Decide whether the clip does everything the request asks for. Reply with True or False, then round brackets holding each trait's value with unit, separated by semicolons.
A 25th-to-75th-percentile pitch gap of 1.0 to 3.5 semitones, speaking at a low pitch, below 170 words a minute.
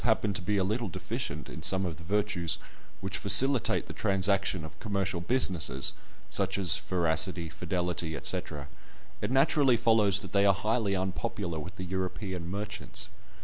True (2.9 semitones; 95 Hz; 155 wpm)